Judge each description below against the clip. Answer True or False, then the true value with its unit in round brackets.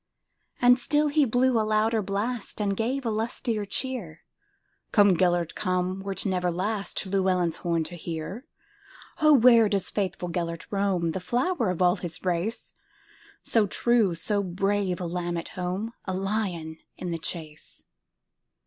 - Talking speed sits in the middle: False (125 wpm)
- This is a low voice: False (195 Hz)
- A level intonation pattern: False (4.3 semitones)